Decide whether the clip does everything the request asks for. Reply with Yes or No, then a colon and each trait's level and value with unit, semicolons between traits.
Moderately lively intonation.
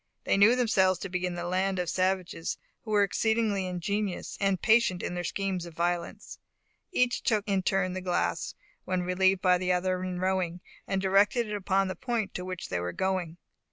No: narrow, 1.9 semitones